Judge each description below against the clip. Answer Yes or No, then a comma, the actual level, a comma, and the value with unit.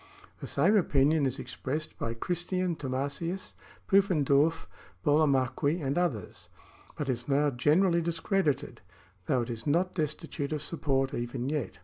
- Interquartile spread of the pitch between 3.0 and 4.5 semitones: Yes, average, 4.1 semitones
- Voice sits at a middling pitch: Yes, medium, 145 Hz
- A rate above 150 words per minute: No, average, 140 wpm